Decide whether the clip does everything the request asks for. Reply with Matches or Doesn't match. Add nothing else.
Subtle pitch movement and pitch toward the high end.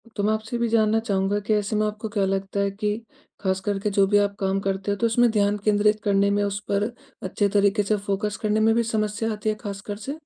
Matches